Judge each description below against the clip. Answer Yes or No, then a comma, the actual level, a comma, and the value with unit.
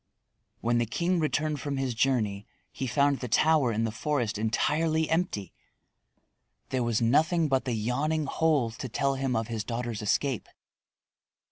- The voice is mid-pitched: No, low, 130 Hz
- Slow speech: No, average, 155 wpm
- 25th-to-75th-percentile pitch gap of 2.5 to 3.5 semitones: No, average, 4.9 semitones